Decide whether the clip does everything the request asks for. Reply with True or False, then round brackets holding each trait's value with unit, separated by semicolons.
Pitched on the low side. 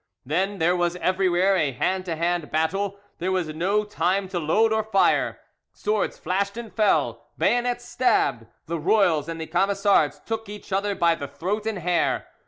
False (190 Hz)